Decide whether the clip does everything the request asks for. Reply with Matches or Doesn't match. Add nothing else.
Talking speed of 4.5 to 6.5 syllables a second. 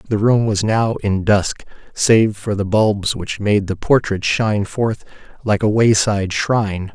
Doesn't match